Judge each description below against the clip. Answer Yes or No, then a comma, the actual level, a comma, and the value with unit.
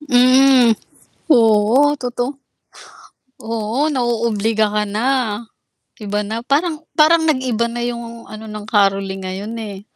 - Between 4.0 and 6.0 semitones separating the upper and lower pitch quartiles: No, average, 3.5 semitones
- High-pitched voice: Yes, high, 230 Hz